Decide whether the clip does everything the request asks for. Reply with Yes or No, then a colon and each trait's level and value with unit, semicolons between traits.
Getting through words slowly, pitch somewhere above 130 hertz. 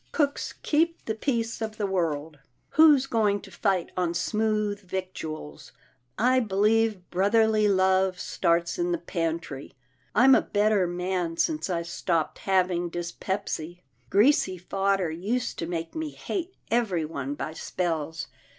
Yes: slow, 130 wpm; high, 190 Hz